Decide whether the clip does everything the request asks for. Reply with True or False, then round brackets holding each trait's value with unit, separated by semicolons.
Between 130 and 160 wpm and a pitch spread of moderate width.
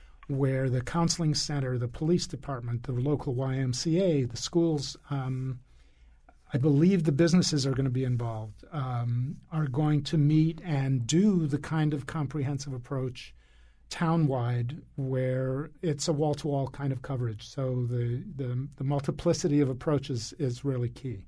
True (150 wpm; 3.3 semitones)